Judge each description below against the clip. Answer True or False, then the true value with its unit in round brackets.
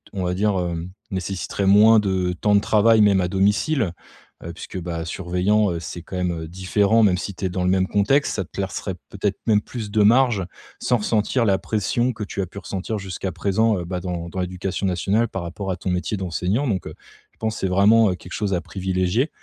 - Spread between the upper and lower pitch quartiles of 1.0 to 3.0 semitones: True (2.6 semitones)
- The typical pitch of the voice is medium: False (95 Hz)